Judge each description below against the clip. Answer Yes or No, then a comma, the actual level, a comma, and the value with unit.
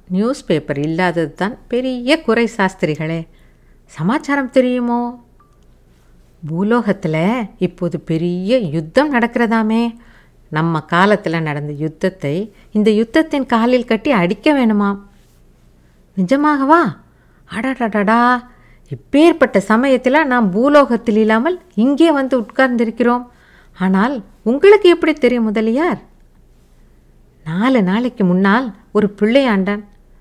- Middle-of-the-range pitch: No, high, 225 Hz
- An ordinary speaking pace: Yes, average, 85 wpm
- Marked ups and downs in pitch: Yes, wide, 5.8 semitones